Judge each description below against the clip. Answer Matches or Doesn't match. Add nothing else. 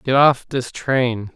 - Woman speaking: Doesn't match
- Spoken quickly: Doesn't match